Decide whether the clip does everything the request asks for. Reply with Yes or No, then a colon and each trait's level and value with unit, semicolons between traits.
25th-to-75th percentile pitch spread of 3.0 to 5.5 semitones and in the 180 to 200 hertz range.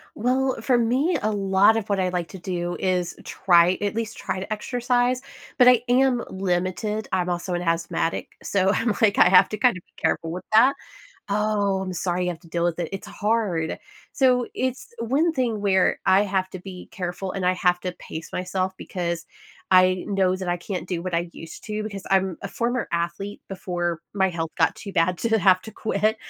Yes: average, 3.4 semitones; high, 190 Hz